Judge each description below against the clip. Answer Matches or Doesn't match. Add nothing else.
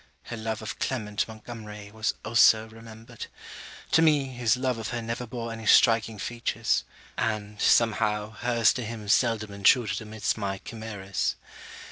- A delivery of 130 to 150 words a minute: Matches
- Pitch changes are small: Matches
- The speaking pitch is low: Matches